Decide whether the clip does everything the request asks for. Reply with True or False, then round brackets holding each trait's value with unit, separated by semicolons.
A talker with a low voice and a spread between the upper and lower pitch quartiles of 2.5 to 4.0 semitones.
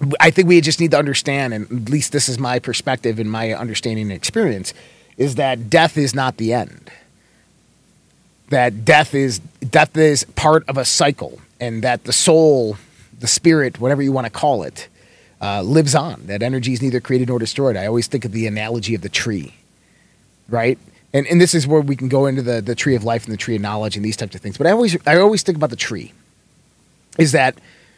False (125 Hz; 4.5 semitones)